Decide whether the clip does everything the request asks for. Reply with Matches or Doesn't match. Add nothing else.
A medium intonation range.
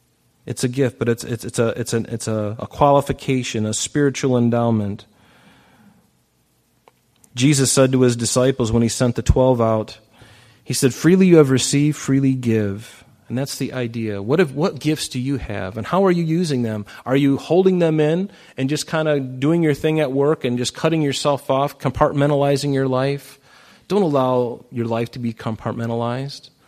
Matches